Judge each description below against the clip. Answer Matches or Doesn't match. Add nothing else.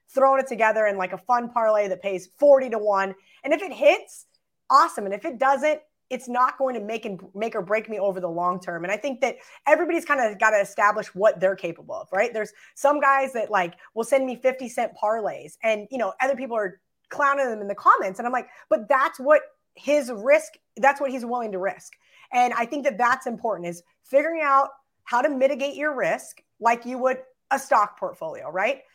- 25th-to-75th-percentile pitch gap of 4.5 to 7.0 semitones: Matches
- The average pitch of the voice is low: Doesn't match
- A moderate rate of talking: Doesn't match